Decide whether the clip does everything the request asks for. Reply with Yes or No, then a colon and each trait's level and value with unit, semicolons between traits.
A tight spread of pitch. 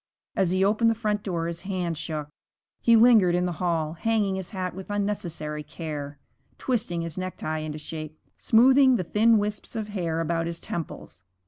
No: average, 4.3 semitones